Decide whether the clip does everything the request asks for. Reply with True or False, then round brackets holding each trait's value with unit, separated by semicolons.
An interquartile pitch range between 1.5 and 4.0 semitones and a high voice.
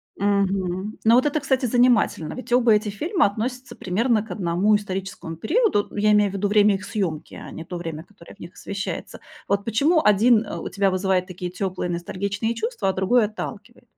True (3.6 semitones; 205 Hz)